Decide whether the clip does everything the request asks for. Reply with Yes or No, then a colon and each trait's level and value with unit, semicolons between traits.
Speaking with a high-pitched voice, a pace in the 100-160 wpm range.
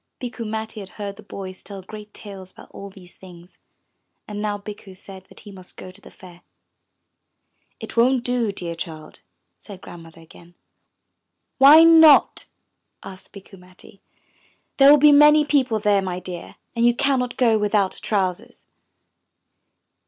Yes: high, 205 Hz; average, 150 wpm